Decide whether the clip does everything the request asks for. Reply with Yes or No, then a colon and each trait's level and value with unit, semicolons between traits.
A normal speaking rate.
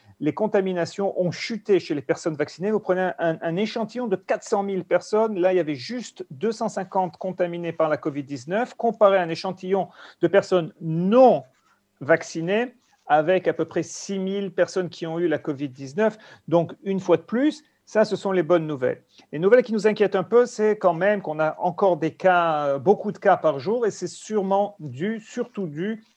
No: fast, 195 wpm